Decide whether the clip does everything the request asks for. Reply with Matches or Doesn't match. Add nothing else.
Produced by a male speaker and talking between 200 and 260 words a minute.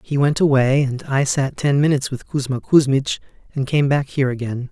Matches